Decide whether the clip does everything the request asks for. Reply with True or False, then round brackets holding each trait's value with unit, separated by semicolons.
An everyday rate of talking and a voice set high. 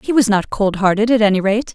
False (275 wpm; 210 Hz)